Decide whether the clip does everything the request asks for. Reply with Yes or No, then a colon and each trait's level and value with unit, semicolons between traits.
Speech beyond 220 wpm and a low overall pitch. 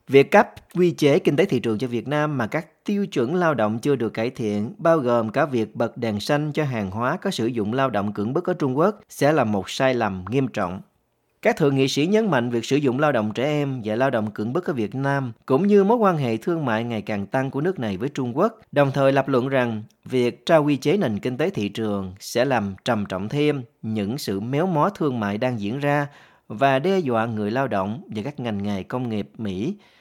Yes: fast, 250 wpm; low, 130 Hz